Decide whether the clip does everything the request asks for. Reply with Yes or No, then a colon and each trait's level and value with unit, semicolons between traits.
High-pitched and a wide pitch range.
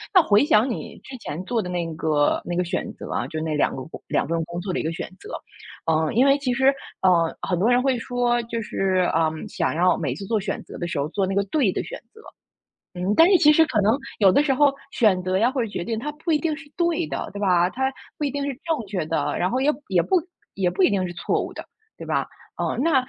Yes: high, 205 Hz; wide, 7.1 semitones